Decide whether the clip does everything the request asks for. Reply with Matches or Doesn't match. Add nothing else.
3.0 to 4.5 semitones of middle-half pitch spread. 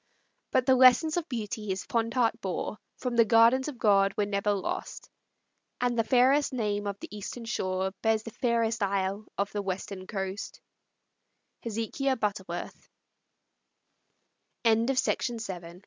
Matches